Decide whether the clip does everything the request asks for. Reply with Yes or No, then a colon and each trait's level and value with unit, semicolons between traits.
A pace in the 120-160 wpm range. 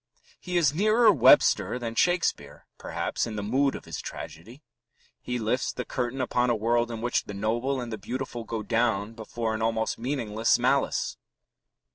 No: average, 170 wpm